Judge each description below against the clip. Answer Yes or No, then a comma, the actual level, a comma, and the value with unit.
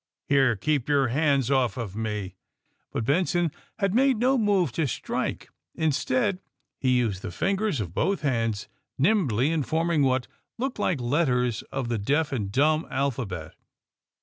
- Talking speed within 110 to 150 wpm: No, average, 160 wpm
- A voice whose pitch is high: No, medium, 140 Hz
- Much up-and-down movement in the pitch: Yes, wide, 6.1 semitones